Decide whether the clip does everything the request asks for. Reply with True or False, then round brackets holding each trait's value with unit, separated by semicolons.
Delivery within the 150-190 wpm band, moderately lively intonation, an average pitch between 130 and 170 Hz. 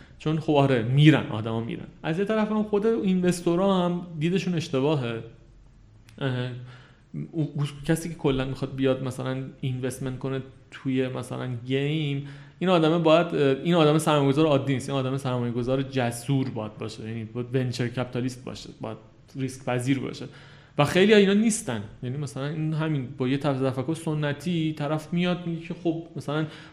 True (155 wpm; 3.6 semitones; 140 Hz)